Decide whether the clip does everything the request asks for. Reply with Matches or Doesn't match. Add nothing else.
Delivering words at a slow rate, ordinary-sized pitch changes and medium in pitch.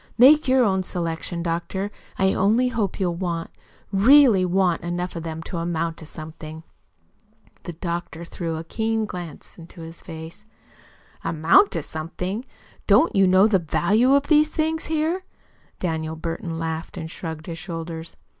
Doesn't match